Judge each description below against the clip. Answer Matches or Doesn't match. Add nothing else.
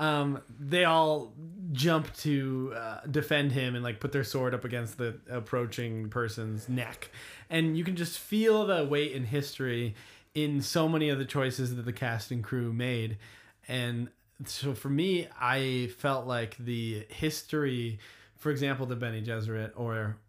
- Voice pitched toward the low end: Matches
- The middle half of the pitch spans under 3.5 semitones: Doesn't match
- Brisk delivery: Doesn't match